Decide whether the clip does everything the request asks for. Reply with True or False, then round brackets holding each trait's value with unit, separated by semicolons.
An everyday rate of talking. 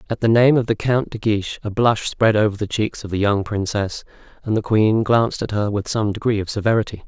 False (245 wpm)